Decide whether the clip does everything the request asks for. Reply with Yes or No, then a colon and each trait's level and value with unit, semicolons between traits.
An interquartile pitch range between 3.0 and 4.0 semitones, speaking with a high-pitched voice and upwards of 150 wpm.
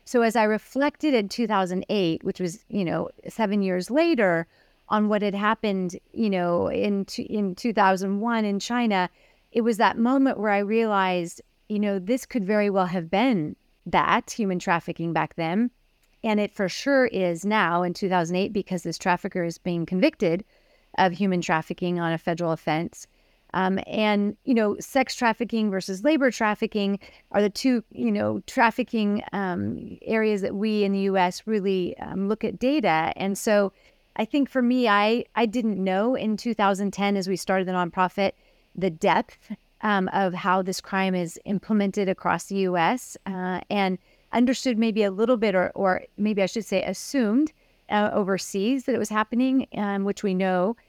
Yes: average, 3.3 semitones; high, 200 Hz; average, 170 wpm